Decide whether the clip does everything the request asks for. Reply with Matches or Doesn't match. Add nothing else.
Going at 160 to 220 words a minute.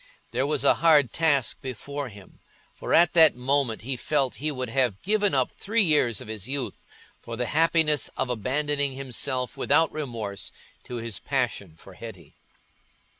Matches